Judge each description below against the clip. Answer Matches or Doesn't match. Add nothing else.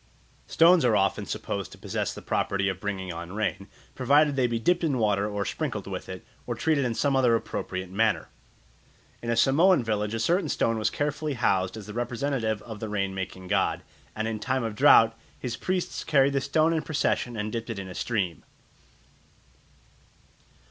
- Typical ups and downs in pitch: Matches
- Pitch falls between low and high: Doesn't match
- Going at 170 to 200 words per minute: Matches